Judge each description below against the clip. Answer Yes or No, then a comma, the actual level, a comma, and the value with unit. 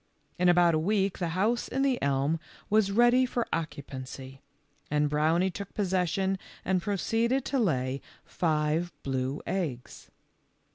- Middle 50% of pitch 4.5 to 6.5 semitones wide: Yes, wide, 5.4 semitones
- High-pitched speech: No, medium, 175 Hz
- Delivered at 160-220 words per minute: No, slow, 135 wpm